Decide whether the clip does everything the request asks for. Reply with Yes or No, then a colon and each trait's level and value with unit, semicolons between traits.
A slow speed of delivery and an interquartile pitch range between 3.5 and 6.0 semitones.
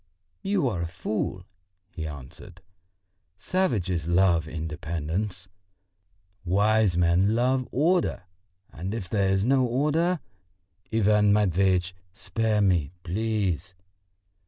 Yes: slow, 100 wpm; average, 4.5 semitones